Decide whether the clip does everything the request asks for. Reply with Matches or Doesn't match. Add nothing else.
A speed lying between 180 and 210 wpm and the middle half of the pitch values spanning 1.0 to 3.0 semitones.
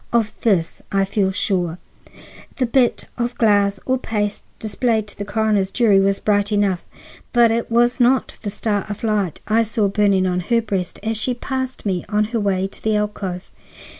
Matches